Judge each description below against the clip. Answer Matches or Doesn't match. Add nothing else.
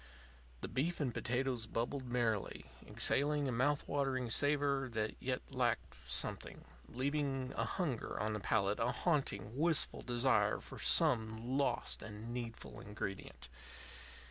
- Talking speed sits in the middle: Doesn't match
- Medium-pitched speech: Doesn't match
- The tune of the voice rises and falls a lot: Doesn't match